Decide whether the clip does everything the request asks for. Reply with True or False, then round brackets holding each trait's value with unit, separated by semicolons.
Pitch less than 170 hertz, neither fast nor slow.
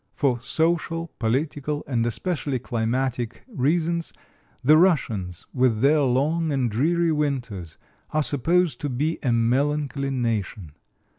False (140 Hz; 120 wpm)